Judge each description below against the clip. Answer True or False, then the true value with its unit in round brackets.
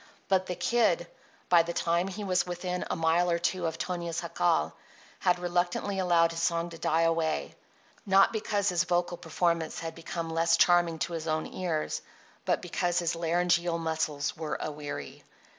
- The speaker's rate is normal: True (165 wpm)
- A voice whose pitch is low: False (170 Hz)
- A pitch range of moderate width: False (1.5 semitones)